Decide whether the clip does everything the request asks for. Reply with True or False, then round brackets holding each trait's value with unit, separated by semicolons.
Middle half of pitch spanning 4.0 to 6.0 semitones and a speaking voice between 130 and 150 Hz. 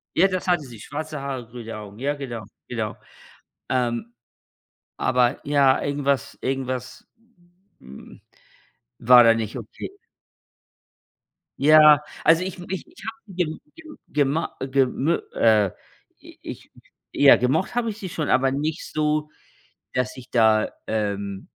True (4.6 semitones; 135 Hz)